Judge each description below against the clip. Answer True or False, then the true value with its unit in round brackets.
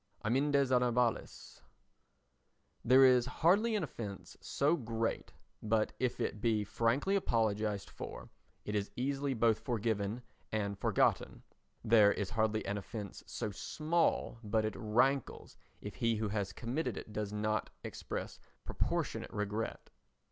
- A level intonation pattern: False (3.4 semitones)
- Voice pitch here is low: True (115 Hz)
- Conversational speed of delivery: False (130 wpm)